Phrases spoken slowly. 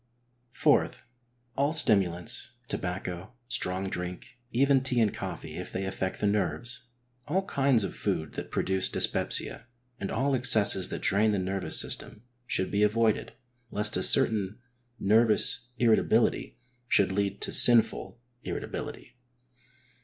Yes: slow, 130 wpm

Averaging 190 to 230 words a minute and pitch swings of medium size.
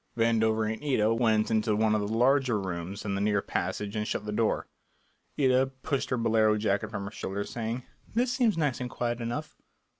Yes: average, 200 wpm; average, 3.2 semitones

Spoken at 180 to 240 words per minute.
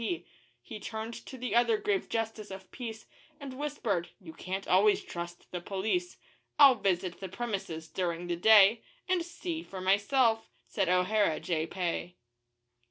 No: average, 155 wpm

